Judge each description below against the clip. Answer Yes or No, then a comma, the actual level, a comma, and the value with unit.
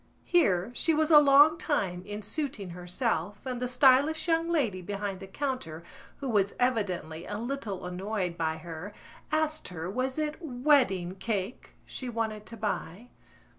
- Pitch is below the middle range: No, high, 220 Hz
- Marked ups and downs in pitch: Yes, wide, 7.0 semitones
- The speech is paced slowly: No, average, 155 wpm